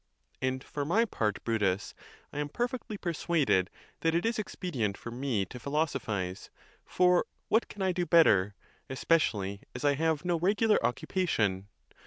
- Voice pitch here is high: No, medium, 145 Hz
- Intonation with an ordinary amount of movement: No, wide, 8.8 semitones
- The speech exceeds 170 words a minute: No, average, 155 wpm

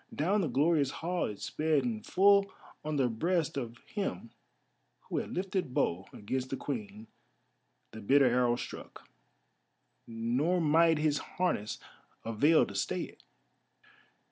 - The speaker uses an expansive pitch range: Yes, wide, 6.4 semitones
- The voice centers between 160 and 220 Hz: No, medium, 140 Hz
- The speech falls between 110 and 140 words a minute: Yes, slow, 135 wpm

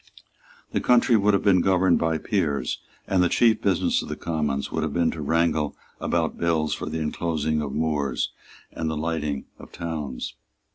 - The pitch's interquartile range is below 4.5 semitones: Yes, average, 2.9 semitones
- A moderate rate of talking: Yes, average, 180 wpm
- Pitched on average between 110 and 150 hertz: No, very low, 80 Hz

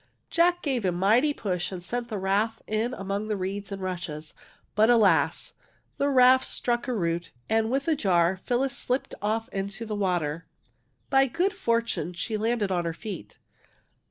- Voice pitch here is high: Yes, high, 215 Hz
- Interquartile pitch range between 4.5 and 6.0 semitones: Yes, average, 4.8 semitones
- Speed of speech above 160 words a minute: Yes, average, 170 wpm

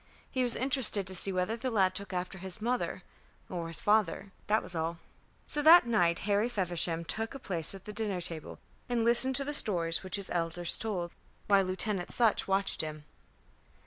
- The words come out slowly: No, average, 190 wpm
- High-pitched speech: Yes, high, 195 Hz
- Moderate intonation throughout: Yes, average, 4.3 semitones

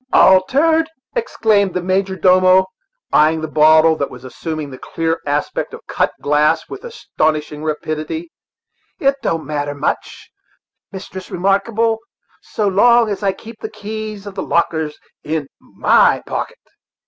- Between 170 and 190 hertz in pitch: Yes, medium, 185 Hz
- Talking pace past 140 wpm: No, slow, 135 wpm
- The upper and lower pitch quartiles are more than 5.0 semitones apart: Yes, wide, 5.4 semitones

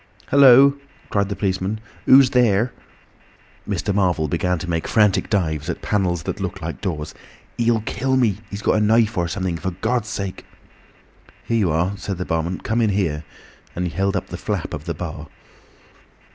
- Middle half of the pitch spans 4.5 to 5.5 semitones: No, average, 4.1 semitones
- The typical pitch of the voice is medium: No, low, 100 Hz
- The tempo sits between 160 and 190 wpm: Yes, average, 175 wpm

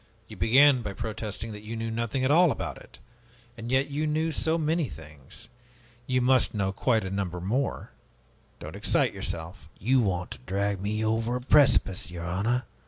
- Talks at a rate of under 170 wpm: No, average, 180 wpm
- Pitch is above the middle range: No, low, 110 Hz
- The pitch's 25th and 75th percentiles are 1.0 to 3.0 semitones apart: No, average, 5.3 semitones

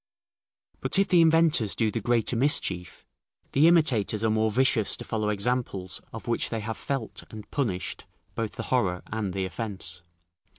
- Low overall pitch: Yes, low, 110 Hz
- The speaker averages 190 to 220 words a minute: No, average, 165 wpm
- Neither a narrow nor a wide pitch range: Yes, average, 4.1 semitones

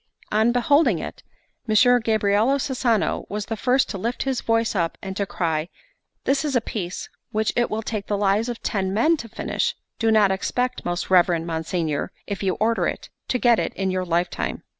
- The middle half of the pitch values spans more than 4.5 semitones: No, average, 4.1 semitones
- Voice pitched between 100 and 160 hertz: No, high, 215 Hz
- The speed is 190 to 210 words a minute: Yes, average, 195 wpm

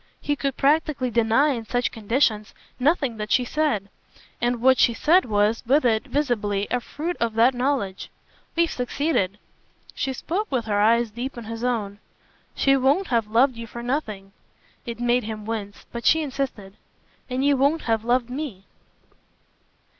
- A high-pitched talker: Yes, high, 245 Hz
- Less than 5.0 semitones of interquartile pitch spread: Yes, average, 3.9 semitones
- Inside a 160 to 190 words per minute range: Yes, average, 165 wpm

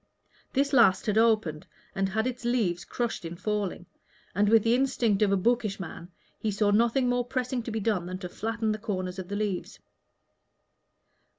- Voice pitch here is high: Yes, high, 215 Hz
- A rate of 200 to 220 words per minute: No, average, 185 wpm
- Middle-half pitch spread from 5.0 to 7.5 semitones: No, average, 3.7 semitones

